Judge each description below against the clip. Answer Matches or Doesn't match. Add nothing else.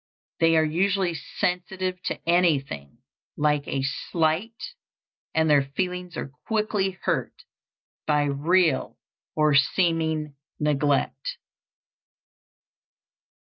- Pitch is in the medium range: Matches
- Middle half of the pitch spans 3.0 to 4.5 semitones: Matches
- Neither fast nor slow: Doesn't match